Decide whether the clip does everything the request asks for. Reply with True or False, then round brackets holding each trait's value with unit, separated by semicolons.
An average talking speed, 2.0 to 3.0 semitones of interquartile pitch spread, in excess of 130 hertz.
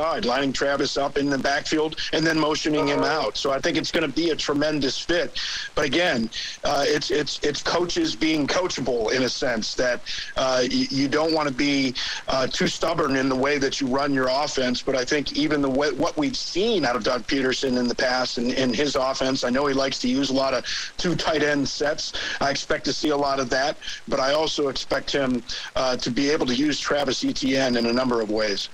False (230 wpm; 2.5 semitones; 140 Hz)